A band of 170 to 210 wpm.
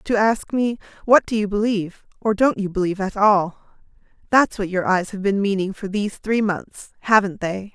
Yes: average, 200 wpm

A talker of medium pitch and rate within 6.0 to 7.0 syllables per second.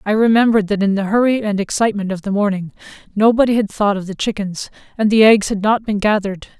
No: high, 205 Hz; 6.5 syllables/s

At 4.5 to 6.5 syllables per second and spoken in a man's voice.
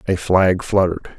Yes: 5.9 syllables/s; male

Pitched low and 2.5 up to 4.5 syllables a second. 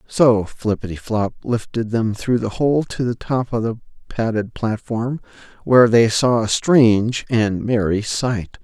Yes: low, 115 Hz; 4.1 syllables/s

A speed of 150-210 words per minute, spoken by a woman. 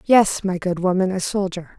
Yes: average, 200 wpm; female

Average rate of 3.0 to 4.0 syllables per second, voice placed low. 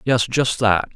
Yes: 3.8 syllables/s; low, 115 Hz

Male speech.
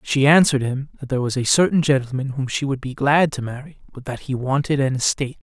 Yes: male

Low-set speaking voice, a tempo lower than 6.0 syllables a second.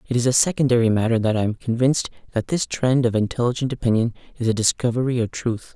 No: low, 120 Hz; 6.6 syllables/s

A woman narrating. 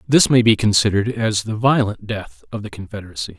No: male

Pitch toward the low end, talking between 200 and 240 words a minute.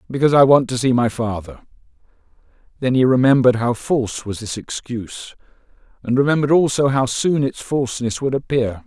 No: low, 125 Hz; average, 160 wpm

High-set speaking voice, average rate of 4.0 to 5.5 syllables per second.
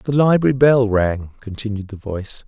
No: low, 115 Hz; 5.0 syllables/s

